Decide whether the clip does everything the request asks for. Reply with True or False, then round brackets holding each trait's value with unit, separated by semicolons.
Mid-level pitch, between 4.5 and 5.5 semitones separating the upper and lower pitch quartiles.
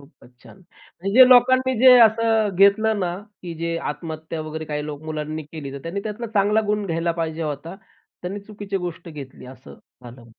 True (170 Hz; 5.1 semitones)